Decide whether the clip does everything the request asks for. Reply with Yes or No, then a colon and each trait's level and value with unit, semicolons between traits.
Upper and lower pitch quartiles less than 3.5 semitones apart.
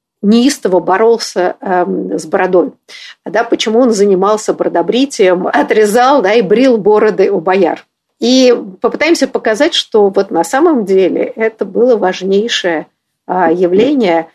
No: average, 4.8 semitones